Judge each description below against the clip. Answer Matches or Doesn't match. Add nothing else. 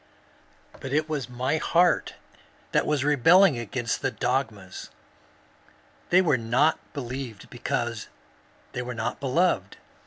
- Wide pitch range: Doesn't match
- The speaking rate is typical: Doesn't match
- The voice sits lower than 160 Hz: Matches